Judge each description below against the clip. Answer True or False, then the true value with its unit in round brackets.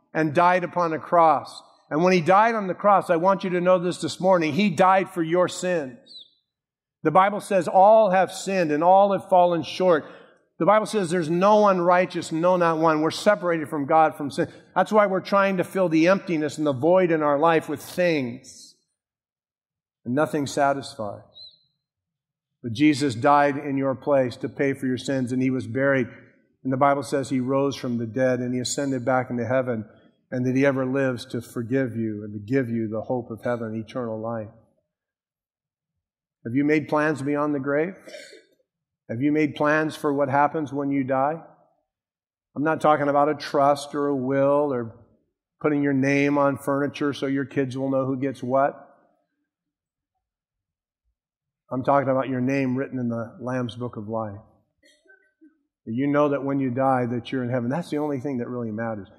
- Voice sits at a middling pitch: True (145 Hz)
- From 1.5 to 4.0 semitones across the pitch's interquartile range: False (4.5 semitones)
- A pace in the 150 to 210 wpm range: True (190 wpm)